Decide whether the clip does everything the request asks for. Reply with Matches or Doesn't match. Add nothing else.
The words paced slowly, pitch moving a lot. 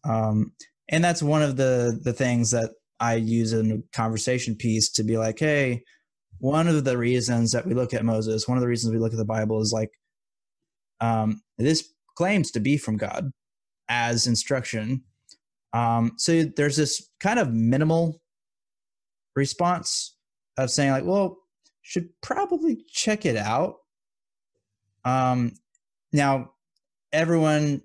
Doesn't match